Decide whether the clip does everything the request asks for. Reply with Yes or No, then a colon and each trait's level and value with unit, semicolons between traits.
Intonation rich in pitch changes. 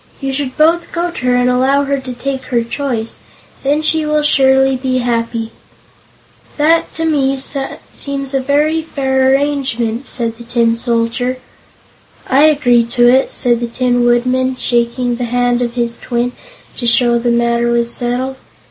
No: narrow, 2.5 semitones